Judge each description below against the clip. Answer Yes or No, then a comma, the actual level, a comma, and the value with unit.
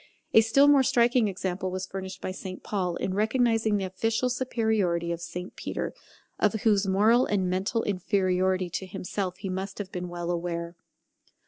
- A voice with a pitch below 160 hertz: No, high, 190 Hz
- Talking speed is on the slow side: No, average, 165 wpm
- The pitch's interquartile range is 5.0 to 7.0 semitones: No, average, 3.3 semitones